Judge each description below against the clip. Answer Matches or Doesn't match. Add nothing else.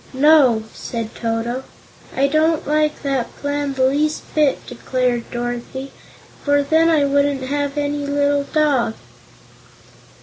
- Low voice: Doesn't match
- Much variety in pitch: Doesn't match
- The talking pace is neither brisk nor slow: Doesn't match